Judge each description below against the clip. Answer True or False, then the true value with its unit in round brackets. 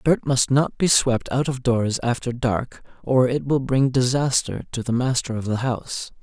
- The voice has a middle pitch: False (125 Hz)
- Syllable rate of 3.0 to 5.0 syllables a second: True (4.5 syllables/s)